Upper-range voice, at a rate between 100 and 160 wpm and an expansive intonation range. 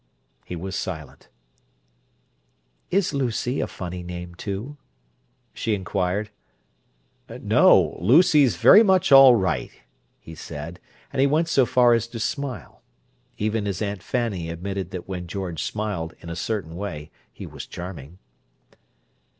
No: low, 100 Hz; slow, 135 wpm; wide, 5.8 semitones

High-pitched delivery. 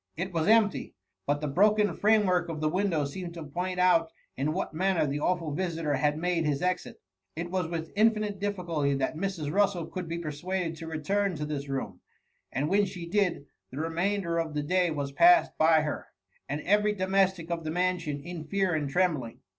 No: medium, 170 Hz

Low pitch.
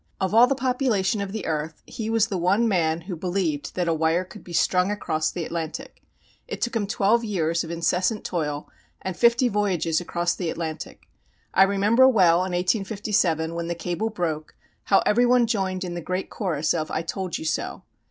No: medium, 185 Hz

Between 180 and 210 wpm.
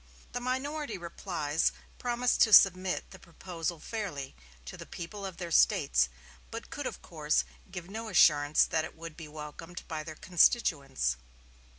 No: average, 155 wpm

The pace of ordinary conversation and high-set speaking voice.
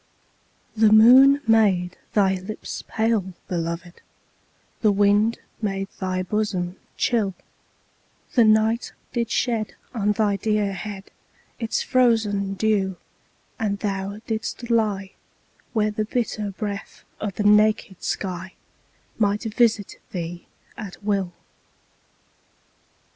No: slow, 110 wpm; high, 210 Hz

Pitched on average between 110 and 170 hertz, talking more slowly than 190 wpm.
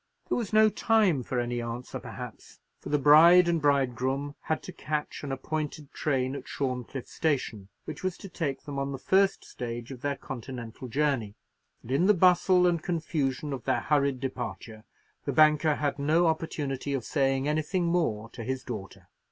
Yes: medium, 140 Hz; average, 175 wpm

